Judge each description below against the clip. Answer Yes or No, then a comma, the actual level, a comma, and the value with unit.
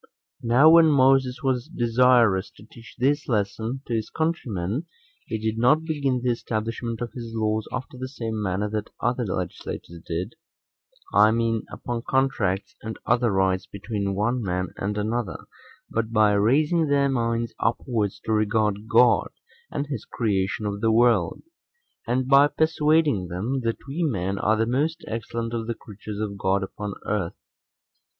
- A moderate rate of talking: Yes, average, 155 wpm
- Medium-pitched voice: No, low, 115 Hz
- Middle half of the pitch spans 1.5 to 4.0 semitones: Yes, average, 3.7 semitones